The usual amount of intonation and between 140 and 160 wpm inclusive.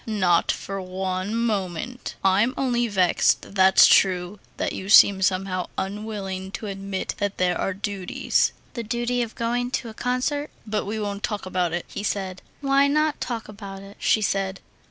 No: average, 3.4 semitones; average, 170 wpm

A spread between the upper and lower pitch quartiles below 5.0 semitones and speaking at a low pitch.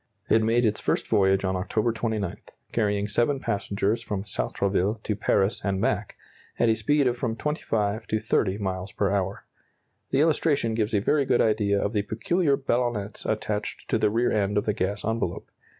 Yes: average, 2.7 semitones; low, 105 Hz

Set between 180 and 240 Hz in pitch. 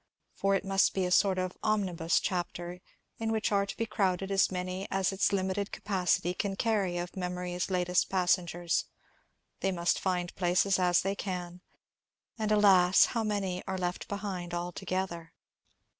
Yes: medium, 185 Hz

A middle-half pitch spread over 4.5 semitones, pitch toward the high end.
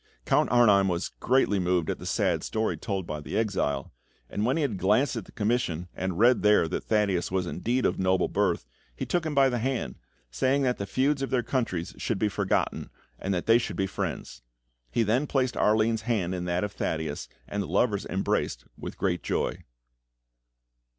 No: average, 5.1 semitones; low, 105 Hz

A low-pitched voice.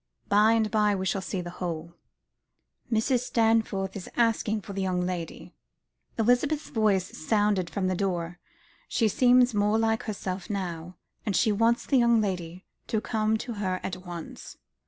No: high, 205 Hz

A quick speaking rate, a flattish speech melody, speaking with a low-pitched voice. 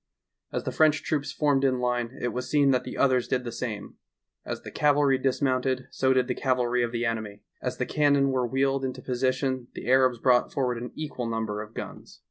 Yes: fast, 215 wpm; narrow, 1.9 semitones; low, 130 Hz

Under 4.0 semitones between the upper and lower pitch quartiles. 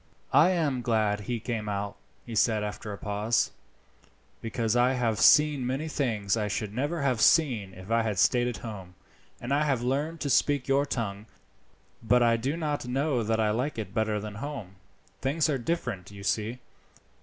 No: average, 4.5 semitones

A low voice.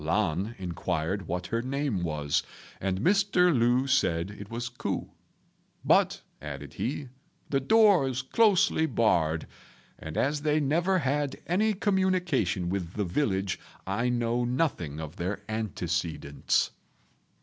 Yes: low, 120 Hz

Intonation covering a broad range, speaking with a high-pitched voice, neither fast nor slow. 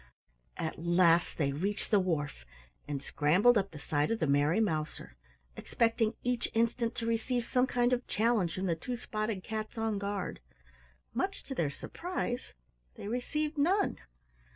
Yes: wide, 6.5 semitones; high, 210 Hz; average, 155 wpm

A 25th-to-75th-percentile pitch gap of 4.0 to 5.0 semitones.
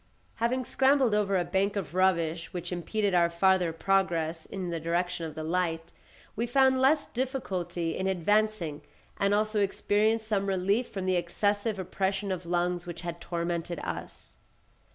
No: average, 3.4 semitones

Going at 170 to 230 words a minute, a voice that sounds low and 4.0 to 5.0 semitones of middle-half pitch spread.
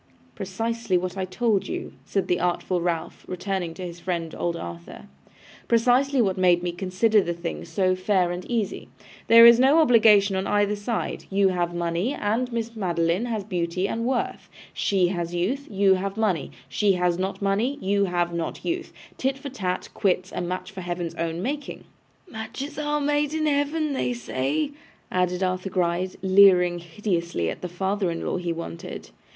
No: average, 175 wpm; high, 190 Hz; average, 4.5 semitones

